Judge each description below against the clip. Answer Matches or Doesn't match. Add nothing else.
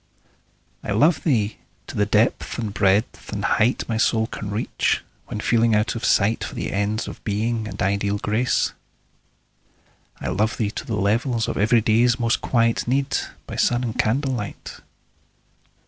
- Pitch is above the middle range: Doesn't match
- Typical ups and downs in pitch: Doesn't match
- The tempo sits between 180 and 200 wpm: Doesn't match